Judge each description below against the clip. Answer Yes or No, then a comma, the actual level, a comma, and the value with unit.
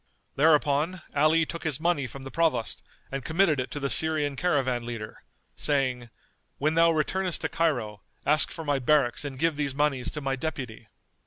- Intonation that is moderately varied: Yes, average, 3.3 semitones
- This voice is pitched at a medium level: Yes, medium, 145 Hz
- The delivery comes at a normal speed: Yes, average, 175 wpm